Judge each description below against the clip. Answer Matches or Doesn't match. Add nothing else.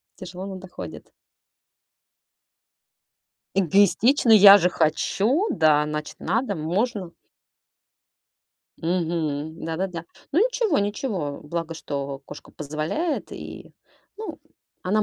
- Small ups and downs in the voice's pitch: Doesn't match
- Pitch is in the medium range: Matches